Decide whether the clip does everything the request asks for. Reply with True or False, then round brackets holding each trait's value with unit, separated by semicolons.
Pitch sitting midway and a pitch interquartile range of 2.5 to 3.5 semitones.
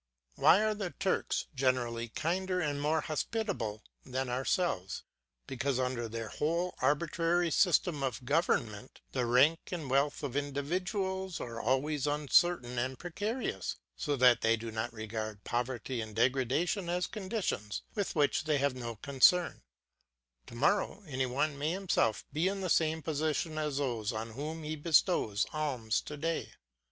False (145 Hz; 5.6 semitones)